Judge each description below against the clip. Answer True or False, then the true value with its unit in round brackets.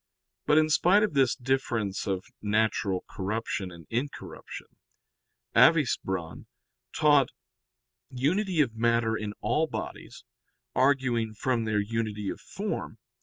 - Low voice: True (115 Hz)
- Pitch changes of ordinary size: True (4.9 semitones)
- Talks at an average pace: False (115 wpm)